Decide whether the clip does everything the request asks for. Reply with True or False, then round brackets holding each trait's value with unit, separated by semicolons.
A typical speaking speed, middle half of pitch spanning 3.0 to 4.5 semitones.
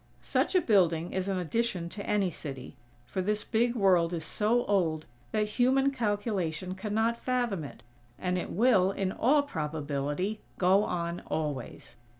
False (155 wpm; 4.9 semitones)